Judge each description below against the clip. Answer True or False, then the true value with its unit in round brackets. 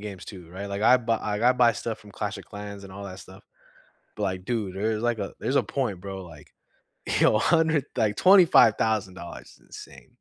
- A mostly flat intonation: False (3.0 semitones)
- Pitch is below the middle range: True (105 Hz)